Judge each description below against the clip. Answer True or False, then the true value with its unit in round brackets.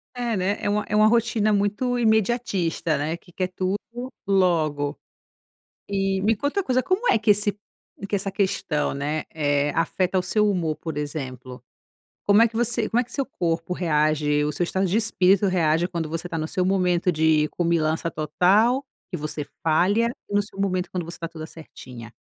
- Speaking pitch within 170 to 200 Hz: True (185 Hz)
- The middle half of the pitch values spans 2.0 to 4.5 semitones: False (4.9 semitones)